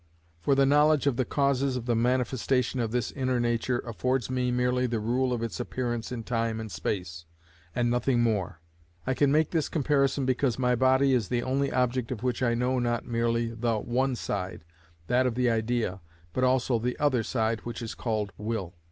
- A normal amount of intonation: No, narrow, 2.1 semitones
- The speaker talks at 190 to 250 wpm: Yes, average, 195 wpm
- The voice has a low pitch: Yes, low, 125 Hz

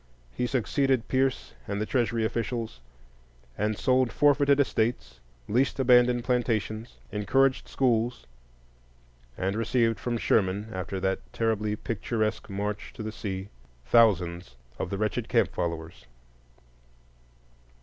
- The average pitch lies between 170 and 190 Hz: No, low, 110 Hz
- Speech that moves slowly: Yes, slow, 115 wpm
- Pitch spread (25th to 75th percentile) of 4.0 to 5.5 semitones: No, average, 3.5 semitones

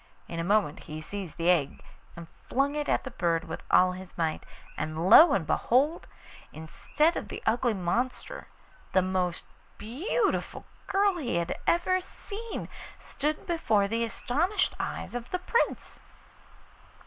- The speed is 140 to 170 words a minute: Yes, average, 150 wpm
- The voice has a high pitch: Yes, high, 225 Hz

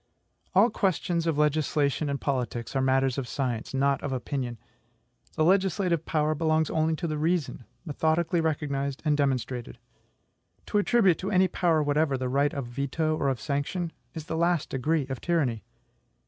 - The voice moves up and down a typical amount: Yes, average, 3.4 semitones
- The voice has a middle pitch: Yes, medium, 150 Hz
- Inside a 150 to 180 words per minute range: Yes, average, 160 wpm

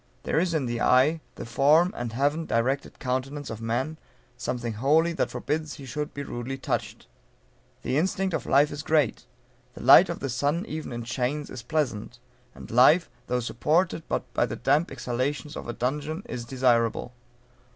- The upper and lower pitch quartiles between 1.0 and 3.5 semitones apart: No, average, 4.2 semitones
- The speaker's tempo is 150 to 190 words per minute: Yes, average, 175 wpm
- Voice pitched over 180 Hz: No, low, 135 Hz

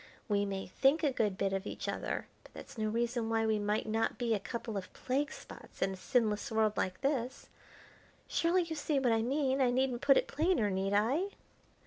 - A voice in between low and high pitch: No, high, 230 Hz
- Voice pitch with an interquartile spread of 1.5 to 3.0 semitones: No, average, 4.5 semitones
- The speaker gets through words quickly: Yes, fast, 210 wpm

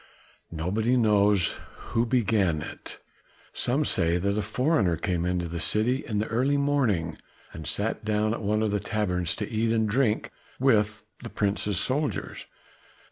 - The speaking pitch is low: Yes, low, 105 Hz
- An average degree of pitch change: Yes, average, 3.7 semitones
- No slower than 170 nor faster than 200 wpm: No, average, 155 wpm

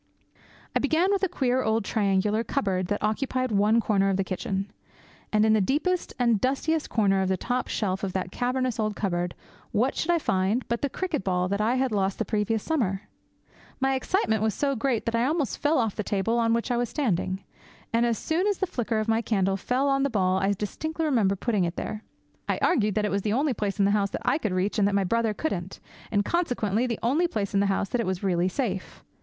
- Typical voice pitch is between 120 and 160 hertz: No, high, 220 Hz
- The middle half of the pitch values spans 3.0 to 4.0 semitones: No, average, 4.6 semitones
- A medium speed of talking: No, fast, 230 wpm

